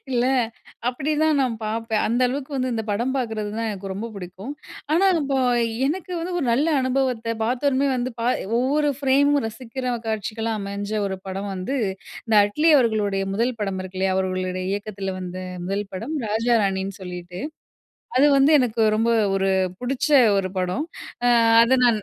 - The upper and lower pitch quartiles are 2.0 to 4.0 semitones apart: No, average, 4.8 semitones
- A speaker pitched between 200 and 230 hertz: Yes, high, 225 Hz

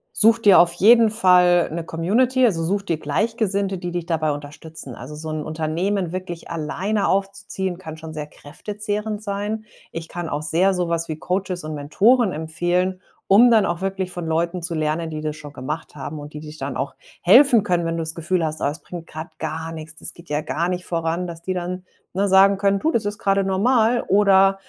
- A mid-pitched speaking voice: Yes, medium, 175 Hz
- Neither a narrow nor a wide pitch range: Yes, average, 3.7 semitones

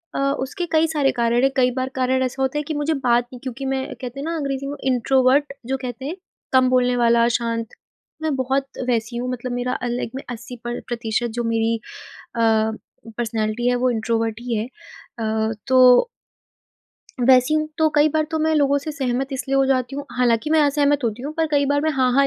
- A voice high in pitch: Yes, very high, 255 Hz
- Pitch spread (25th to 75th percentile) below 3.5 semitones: Yes, average, 2.8 semitones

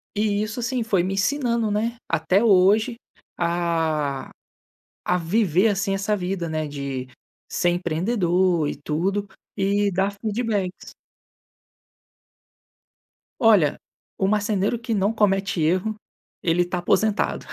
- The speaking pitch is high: Yes, high, 195 Hz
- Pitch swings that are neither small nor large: Yes, average, 3.7 semitones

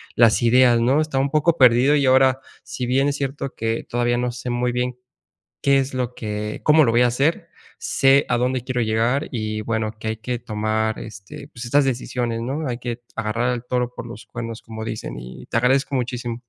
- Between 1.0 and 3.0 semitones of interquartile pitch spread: Yes, narrow, 2.5 semitones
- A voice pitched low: Yes, low, 120 Hz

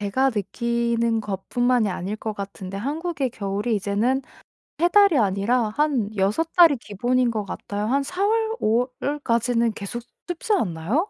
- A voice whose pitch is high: Yes, high, 235 Hz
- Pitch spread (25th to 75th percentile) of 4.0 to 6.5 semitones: Yes, average, 5.3 semitones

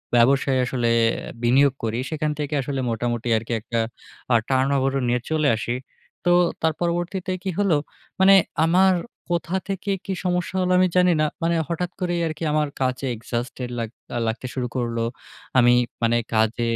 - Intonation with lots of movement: Yes, wide, 6.4 semitones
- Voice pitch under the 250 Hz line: Yes, medium, 140 Hz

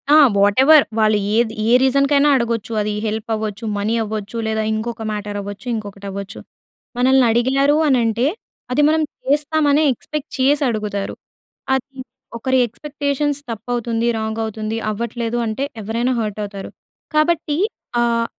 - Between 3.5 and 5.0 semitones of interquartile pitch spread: Yes, average, 4.1 semitones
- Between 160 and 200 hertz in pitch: No, high, 235 Hz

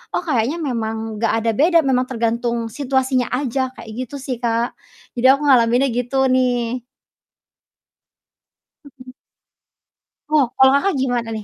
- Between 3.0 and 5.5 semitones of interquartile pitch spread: No, narrow, 2.5 semitones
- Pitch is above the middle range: Yes, very high, 250 Hz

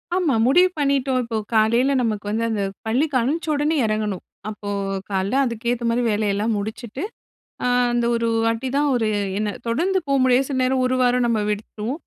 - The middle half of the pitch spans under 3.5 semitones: No, average, 3.8 semitones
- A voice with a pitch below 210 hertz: No, high, 240 Hz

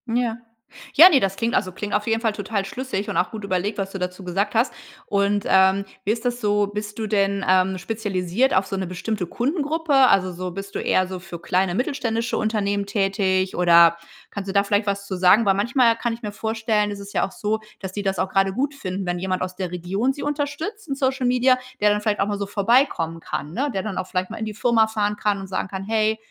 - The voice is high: Yes, high, 205 Hz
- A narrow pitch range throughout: No, average, 3.0 semitones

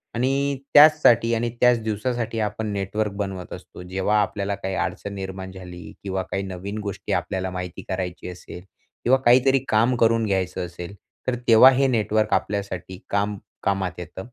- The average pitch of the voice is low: Yes, low, 100 Hz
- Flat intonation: No, average, 3.6 semitones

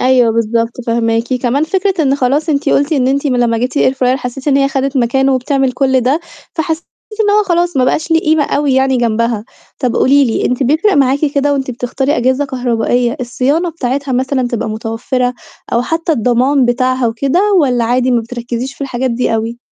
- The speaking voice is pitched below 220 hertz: No, very high, 260 Hz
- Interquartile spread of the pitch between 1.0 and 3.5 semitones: Yes, average, 2.7 semitones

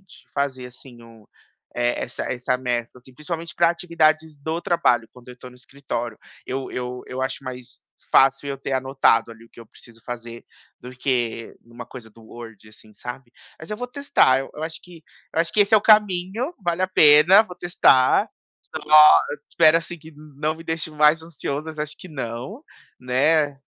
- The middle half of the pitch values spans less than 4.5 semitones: No, average, 4.8 semitones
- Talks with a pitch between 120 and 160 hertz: Yes, medium, 140 Hz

